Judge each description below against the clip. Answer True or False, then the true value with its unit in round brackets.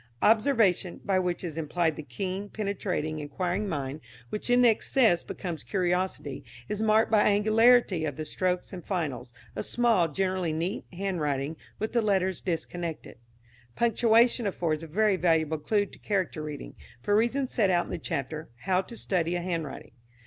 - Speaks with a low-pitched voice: False (185 Hz)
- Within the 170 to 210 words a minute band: False (160 wpm)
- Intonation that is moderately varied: True (4.7 semitones)